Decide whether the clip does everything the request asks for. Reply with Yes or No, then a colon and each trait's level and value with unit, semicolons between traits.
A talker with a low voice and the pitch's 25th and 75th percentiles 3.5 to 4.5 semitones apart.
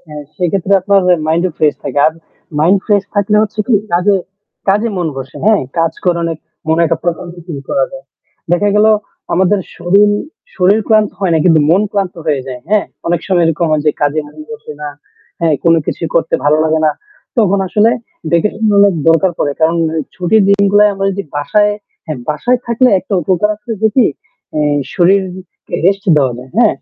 No: medium, 185 Hz; average, 4.2 semitones